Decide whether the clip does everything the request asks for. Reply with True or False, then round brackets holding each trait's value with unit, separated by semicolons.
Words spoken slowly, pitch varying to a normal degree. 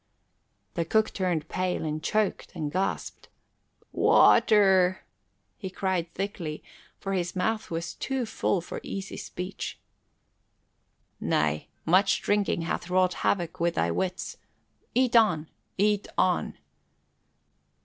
True (115 wpm; 3.2 semitones)